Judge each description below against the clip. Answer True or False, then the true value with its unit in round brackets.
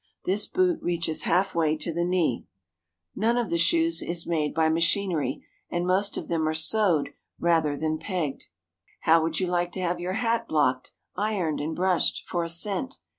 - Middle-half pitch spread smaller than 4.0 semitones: True (3.5 semitones)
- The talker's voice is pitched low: False (175 Hz)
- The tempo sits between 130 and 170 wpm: False (180 wpm)